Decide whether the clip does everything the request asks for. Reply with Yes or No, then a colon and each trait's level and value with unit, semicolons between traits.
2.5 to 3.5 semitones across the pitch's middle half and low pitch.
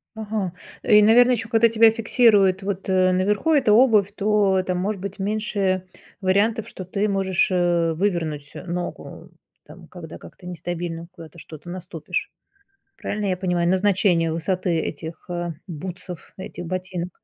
No: average, 3.0 semitones; medium, 185 Hz